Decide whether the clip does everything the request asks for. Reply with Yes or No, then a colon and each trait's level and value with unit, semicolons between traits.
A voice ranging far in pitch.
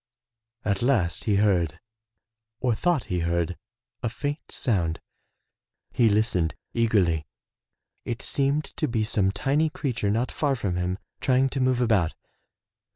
Yes: wide, 6.2 semitones